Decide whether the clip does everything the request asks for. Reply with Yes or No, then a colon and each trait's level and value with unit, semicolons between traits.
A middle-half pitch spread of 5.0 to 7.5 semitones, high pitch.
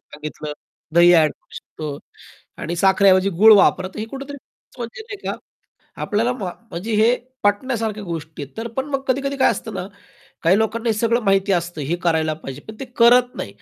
Yes: wide, 5.6 semitones; high, 205 Hz